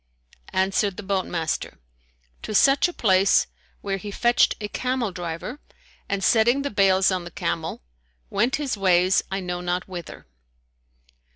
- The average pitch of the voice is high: Yes, high, 195 Hz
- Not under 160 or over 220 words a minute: No, average, 150 wpm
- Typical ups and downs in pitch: Yes, average, 3.4 semitones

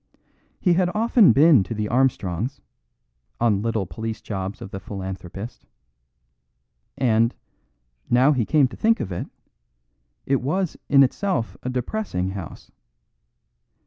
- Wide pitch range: Yes, wide, 6.6 semitones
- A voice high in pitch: No, low, 120 Hz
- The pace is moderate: No, slow, 125 wpm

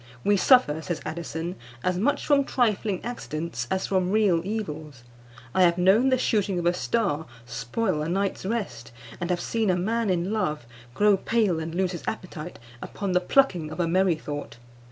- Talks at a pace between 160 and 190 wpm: Yes, average, 175 wpm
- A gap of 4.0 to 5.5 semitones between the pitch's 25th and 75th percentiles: Yes, average, 4.5 semitones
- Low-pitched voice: No, medium, 180 Hz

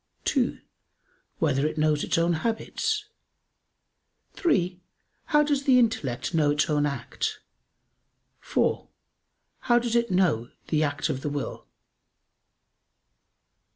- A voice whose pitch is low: No, medium, 170 Hz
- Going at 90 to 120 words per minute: Yes, slow, 115 wpm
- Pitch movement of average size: No, wide, 8.4 semitones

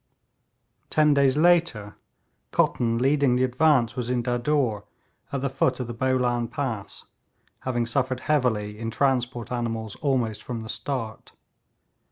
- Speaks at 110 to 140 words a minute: Yes, slow, 135 wpm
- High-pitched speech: No, low, 125 Hz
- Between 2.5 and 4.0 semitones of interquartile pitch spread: Yes, average, 2.9 semitones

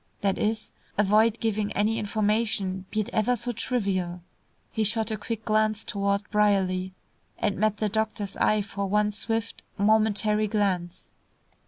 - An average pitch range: No, narrow, 1.5 semitones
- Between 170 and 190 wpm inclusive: No, average, 145 wpm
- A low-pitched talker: No, high, 210 Hz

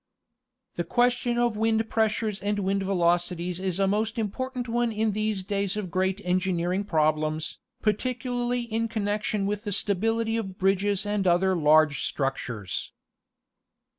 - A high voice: Yes, high, 205 Hz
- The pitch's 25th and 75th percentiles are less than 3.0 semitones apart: No, average, 3.5 semitones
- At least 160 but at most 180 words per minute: No, average, 140 wpm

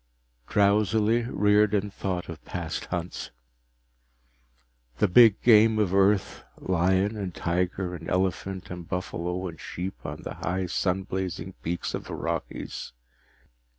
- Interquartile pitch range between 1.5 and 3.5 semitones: Yes, narrow, 2.6 semitones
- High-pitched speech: No, very low, 95 Hz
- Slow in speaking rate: Yes, slow, 130 wpm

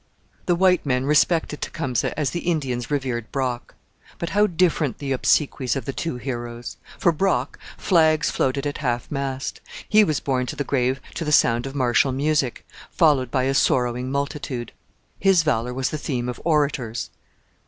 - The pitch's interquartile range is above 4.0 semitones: No, average, 3.6 semitones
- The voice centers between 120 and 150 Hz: Yes, low, 135 Hz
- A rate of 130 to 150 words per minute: No, average, 170 wpm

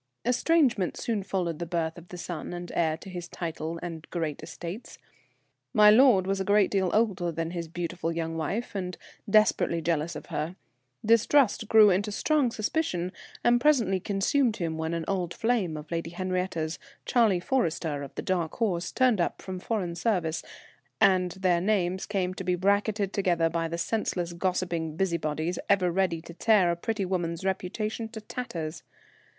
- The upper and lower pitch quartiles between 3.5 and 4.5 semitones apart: Yes, average, 3.8 semitones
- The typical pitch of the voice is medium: Yes, medium, 180 Hz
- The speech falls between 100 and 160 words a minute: No, average, 170 wpm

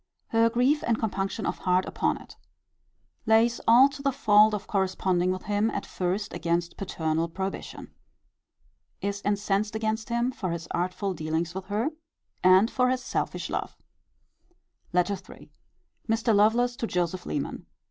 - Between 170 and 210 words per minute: No, average, 145 wpm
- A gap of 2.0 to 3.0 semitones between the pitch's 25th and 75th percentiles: No, average, 3.7 semitones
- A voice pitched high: Yes, high, 205 Hz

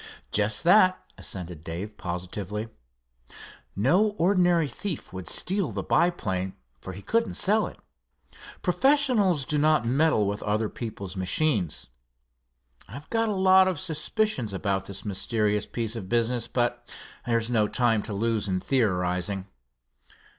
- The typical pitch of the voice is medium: No, low, 115 Hz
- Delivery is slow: Yes, slow, 130 wpm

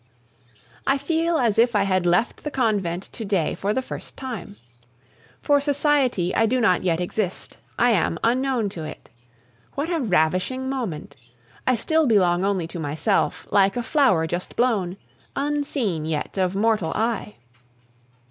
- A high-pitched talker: Yes, high, 215 Hz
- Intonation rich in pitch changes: Yes, wide, 6.3 semitones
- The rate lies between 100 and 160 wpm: Yes, average, 155 wpm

